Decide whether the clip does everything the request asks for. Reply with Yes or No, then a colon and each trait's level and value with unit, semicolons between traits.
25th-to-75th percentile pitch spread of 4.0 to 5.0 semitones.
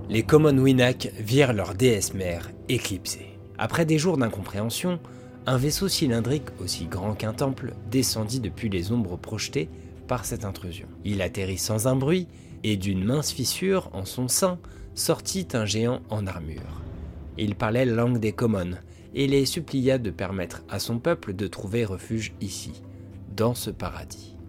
Yes: average, 4.7 semitones